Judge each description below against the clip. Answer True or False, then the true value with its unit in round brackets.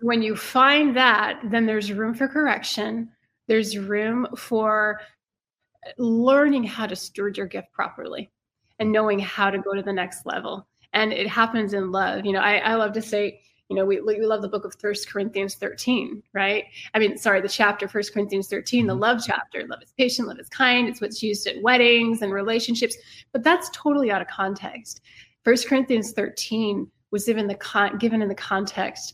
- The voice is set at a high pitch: True (215 Hz)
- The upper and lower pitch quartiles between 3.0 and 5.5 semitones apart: False (2.6 semitones)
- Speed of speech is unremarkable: True (190 wpm)